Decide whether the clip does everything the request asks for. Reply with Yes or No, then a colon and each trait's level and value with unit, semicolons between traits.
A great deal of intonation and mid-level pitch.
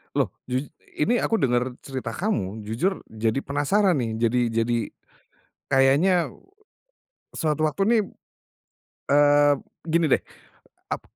Yes: wide, 5.8 semitones; medium, 145 Hz